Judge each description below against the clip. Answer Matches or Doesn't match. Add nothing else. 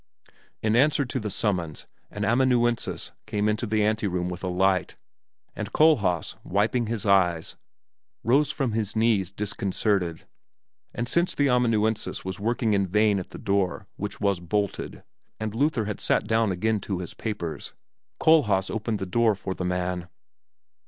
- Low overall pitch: Matches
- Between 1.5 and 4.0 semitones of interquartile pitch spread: Matches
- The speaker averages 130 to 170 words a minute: Matches